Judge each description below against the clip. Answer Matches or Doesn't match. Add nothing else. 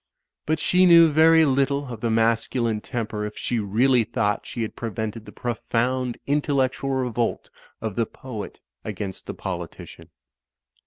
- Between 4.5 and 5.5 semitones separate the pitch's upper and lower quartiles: Doesn't match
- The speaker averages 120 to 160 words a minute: Matches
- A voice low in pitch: Matches